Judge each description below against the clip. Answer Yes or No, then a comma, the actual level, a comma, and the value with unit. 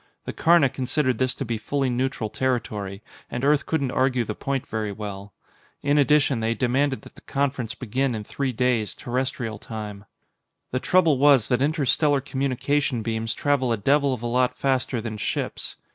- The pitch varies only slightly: No, average, 3.6 semitones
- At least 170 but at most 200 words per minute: Yes, average, 175 wpm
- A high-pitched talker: No, low, 130 Hz